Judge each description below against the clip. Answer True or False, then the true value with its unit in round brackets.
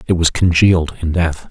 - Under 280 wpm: True (200 wpm)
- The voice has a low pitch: True (85 Hz)